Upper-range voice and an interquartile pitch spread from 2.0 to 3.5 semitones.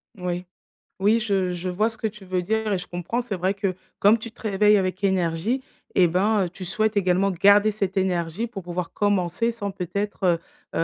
Yes: high, 195 Hz; average, 2.9 semitones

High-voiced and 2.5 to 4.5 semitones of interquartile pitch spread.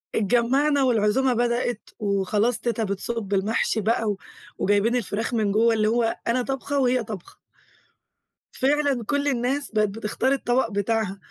Yes: high, 230 Hz; average, 3.2 semitones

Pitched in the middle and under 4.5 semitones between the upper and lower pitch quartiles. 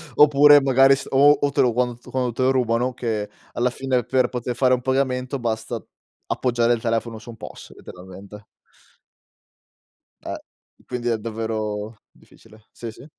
No: low, 120 Hz; average, 2.7 semitones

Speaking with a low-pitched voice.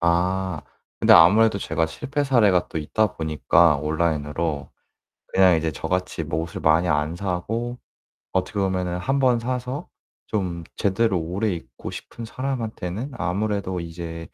Yes: very low, 90 Hz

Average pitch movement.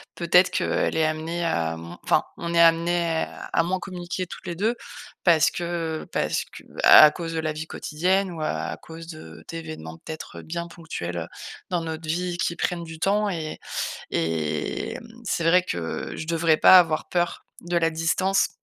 No: narrow, 1.8 semitones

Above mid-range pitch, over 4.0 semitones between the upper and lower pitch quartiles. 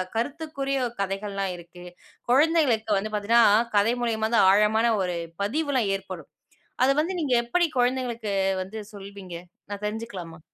Yes: high, 220 Hz; average, 4.5 semitones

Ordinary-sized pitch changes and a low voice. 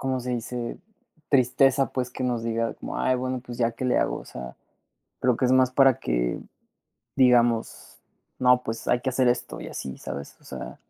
No: narrow, 1.8 semitones; low, 125 Hz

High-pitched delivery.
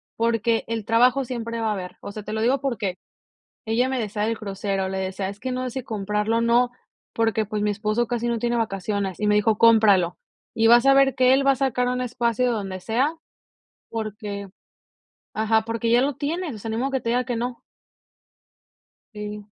Yes: high, 225 Hz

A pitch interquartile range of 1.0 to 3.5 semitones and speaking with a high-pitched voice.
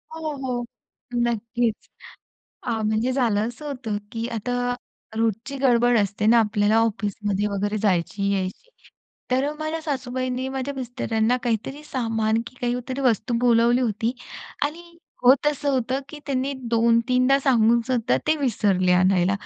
Yes: average, 3.1 semitones; high, 240 Hz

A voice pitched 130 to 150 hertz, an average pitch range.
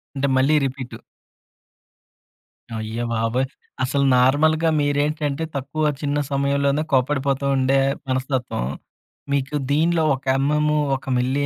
No: medium, 140 Hz; narrow, 2.1 semitones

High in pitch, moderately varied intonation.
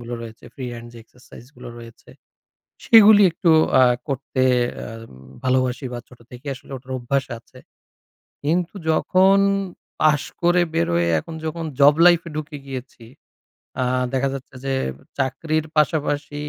No: medium, 140 Hz; average, 4.0 semitones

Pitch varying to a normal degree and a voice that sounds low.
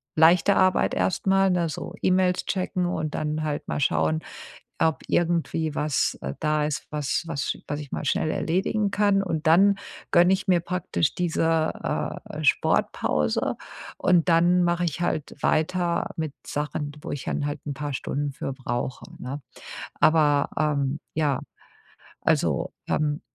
No: average, 3.4 semitones; medium, 160 Hz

